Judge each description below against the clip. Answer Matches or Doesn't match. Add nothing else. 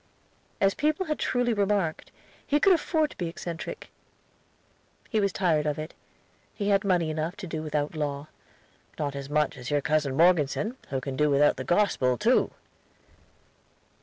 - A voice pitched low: Doesn't match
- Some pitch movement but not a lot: Doesn't match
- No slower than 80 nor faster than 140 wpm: Doesn't match